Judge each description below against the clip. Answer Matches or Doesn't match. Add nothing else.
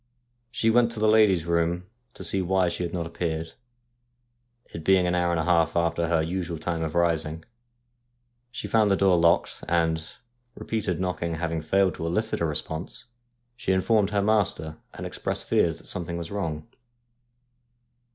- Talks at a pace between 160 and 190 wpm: Matches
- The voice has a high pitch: Doesn't match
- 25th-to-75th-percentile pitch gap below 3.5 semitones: Matches